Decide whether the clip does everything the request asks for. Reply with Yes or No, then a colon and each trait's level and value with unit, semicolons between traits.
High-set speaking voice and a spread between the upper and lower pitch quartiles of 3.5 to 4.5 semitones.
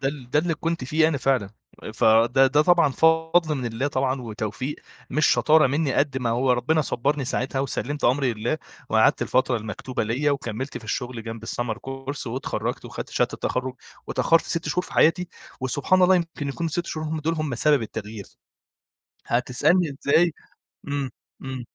No: low, 135 Hz; average, 4.1 semitones